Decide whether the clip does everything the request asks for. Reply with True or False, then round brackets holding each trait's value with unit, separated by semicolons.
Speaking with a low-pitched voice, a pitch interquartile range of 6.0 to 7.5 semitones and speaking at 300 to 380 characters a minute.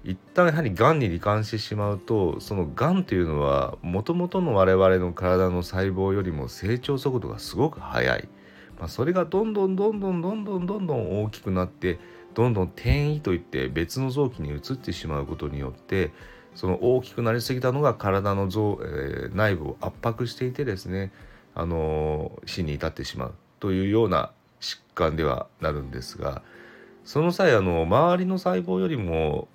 True (100 Hz; 7.2 semitones; 355 characters per minute)